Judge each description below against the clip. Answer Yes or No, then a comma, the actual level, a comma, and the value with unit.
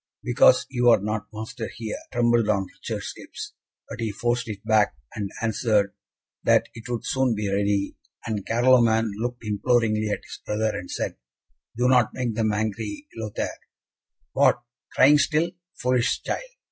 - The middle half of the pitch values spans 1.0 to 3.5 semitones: Yes, narrow, 2.4 semitones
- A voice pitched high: No, low, 110 Hz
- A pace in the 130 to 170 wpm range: Yes, average, 155 wpm